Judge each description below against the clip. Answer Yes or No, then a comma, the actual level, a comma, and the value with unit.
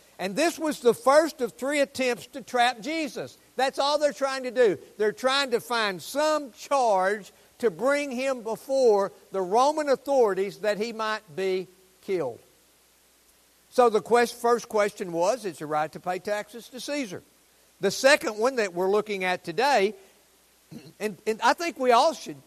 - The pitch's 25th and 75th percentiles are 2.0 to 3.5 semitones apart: No, average, 5.3 semitones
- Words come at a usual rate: Yes, average, 170 wpm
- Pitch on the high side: Yes, high, 235 Hz